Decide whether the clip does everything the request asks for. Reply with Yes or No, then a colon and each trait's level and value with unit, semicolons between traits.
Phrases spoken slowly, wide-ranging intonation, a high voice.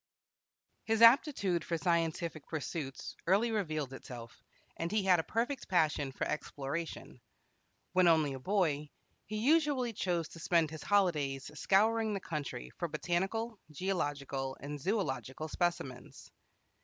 No: slow, 130 wpm; wide, 5.8 semitones; medium, 170 Hz